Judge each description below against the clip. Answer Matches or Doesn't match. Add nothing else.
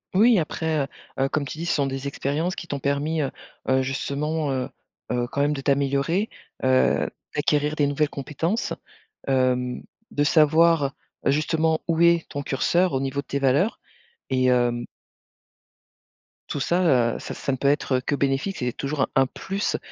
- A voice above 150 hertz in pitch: Doesn't match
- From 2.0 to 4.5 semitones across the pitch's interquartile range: Matches